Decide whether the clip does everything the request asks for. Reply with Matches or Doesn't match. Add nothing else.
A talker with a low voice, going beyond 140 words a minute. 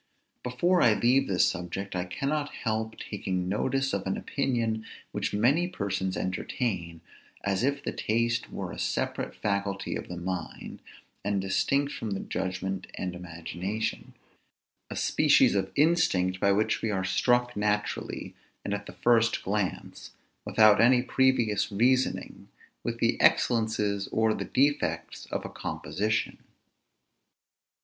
Doesn't match